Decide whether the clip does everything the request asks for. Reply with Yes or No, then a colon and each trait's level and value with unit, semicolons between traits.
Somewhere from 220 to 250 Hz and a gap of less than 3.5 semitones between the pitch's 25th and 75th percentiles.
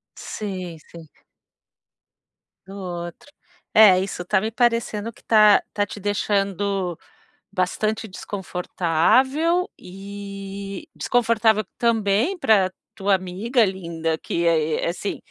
No: high, 200 Hz; average, 3.1 semitones